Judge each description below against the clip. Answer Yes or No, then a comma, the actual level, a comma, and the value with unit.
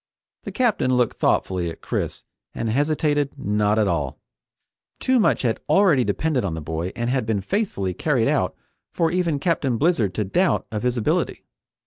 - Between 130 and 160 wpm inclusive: No, average, 170 wpm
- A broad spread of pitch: Yes, wide, 7.5 semitones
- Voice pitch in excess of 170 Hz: No, low, 125 Hz